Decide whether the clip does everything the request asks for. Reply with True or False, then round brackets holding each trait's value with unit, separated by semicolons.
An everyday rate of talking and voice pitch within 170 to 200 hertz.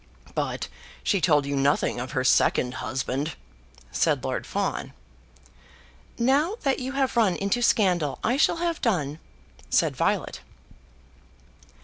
False (125 wpm; 185 Hz)